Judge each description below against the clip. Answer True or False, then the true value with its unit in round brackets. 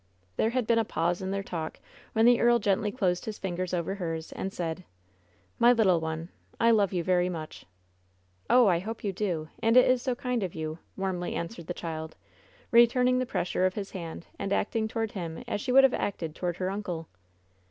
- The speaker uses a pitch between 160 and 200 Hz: True (190 Hz)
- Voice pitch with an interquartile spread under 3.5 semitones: False (4.9 semitones)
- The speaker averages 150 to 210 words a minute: True (205 wpm)